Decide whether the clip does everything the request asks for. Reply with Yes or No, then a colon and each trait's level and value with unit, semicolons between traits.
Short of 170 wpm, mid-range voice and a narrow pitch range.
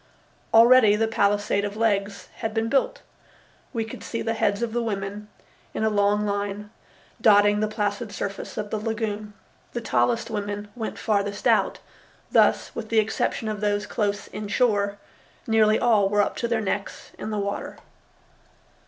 No: average, 160 wpm; high, 210 Hz; narrow, 1.6 semitones